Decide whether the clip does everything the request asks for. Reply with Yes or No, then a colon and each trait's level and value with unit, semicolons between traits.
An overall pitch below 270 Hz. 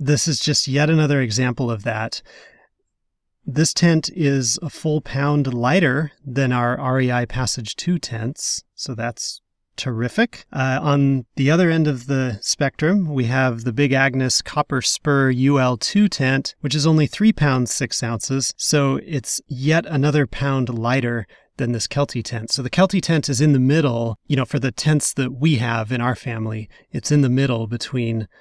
Yes: low, 135 Hz